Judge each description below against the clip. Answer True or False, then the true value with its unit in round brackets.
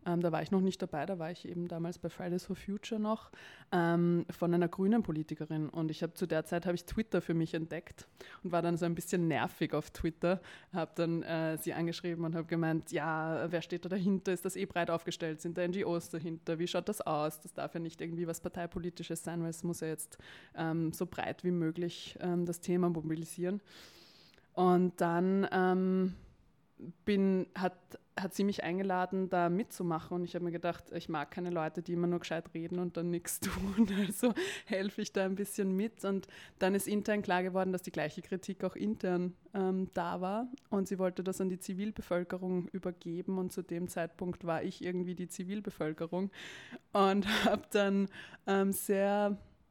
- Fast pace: True (200 wpm)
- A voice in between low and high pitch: True (180 Hz)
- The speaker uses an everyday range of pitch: False (2.1 semitones)